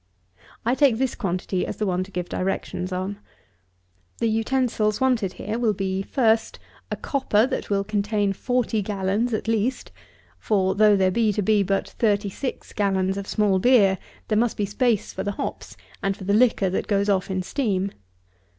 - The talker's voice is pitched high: Yes, high, 205 Hz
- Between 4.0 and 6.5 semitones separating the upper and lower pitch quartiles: No, average, 2.7 semitones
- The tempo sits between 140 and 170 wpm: No, average, 180 wpm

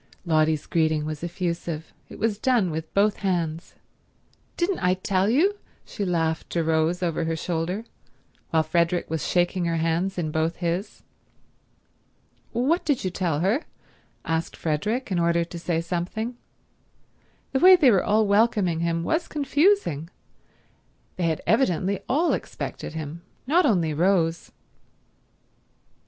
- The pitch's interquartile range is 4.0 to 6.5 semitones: Yes, average, 4.8 semitones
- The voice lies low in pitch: No, medium, 175 Hz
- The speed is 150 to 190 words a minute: No, average, 140 wpm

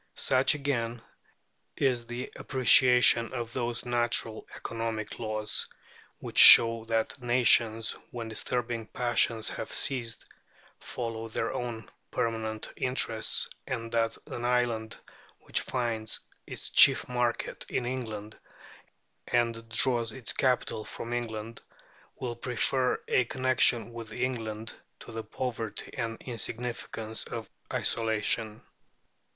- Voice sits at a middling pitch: No, low, 115 Hz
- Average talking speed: No, slow, 110 wpm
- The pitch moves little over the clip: Yes, narrow, 1.6 semitones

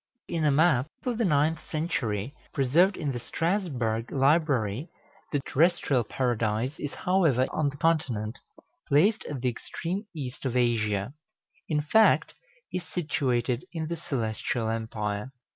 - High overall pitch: No, medium, 140 Hz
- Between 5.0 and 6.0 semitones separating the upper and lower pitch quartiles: Yes, wide, 5.5 semitones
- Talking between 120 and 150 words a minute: Yes, slow, 135 wpm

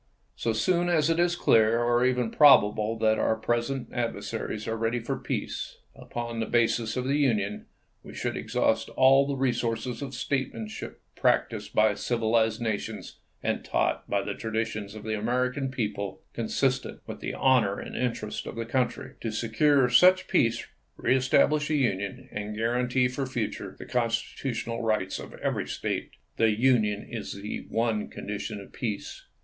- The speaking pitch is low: Yes, low, 115 Hz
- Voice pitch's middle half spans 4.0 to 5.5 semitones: No, average, 3.0 semitones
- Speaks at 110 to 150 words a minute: No, average, 165 wpm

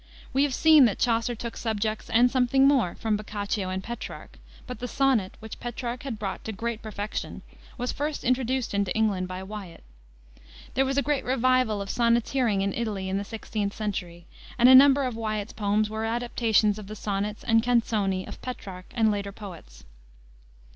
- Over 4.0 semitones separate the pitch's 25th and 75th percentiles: No, average, 3.5 semitones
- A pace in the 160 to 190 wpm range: Yes, average, 180 wpm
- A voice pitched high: Yes, high, 220 Hz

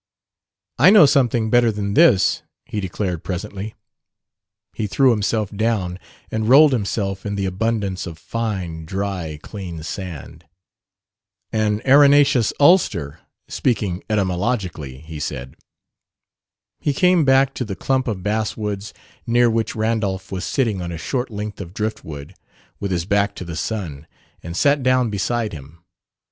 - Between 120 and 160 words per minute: Yes, average, 140 wpm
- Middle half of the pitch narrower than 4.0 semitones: No, average, 4.6 semitones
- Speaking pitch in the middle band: No, low, 105 Hz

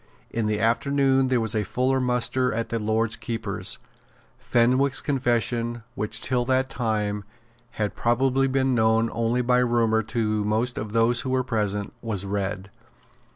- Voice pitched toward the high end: No, low, 115 Hz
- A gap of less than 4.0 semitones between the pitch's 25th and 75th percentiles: Yes, narrow, 2.6 semitones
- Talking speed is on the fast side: No, average, 155 wpm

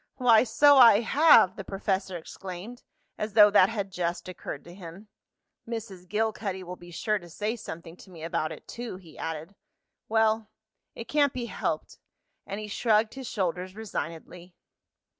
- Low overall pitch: No, high, 200 Hz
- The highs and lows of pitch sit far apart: No, average, 3.8 semitones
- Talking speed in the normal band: Yes, average, 160 wpm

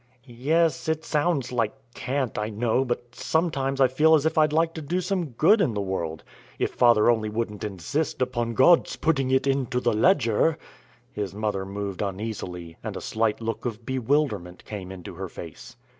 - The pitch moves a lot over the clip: Yes, wide, 6.0 semitones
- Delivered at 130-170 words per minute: No, average, 180 wpm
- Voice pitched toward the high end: No, low, 120 Hz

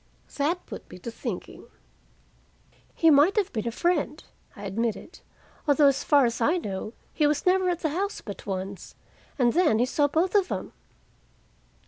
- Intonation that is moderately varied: No, wide, 7.0 semitones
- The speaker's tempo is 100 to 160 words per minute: No, average, 170 wpm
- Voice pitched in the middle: No, very high, 290 Hz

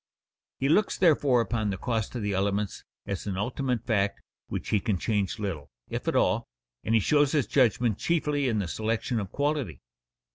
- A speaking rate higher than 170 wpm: Yes, average, 185 wpm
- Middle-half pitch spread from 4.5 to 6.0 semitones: Yes, average, 5.1 semitones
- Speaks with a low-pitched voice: Yes, low, 110 Hz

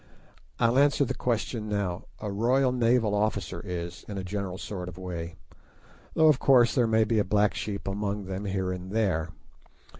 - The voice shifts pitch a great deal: No, average, 3.7 semitones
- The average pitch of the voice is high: No, low, 105 Hz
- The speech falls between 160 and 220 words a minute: Yes, average, 180 wpm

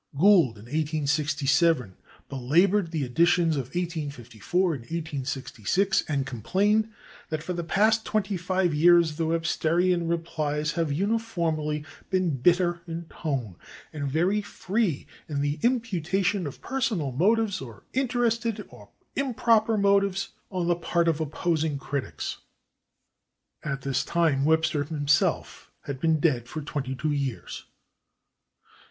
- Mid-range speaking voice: Yes, medium, 165 Hz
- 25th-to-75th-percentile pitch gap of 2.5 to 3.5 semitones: No, average, 4.7 semitones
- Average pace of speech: No, slow, 125 wpm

